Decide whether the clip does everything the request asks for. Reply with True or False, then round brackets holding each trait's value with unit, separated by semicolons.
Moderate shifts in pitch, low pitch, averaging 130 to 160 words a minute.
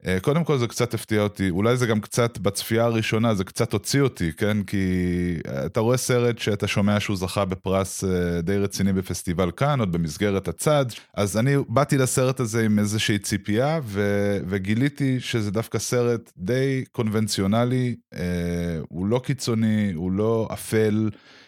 True (3.7 semitones; 105 Hz; 150 wpm)